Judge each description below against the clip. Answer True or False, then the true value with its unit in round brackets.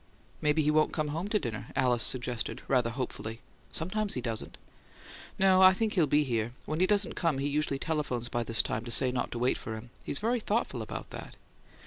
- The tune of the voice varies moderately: False (6.5 semitones)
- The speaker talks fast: True (210 wpm)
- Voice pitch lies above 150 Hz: False (140 Hz)